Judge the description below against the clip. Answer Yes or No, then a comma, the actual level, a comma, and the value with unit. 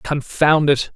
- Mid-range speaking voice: Yes, medium, 145 Hz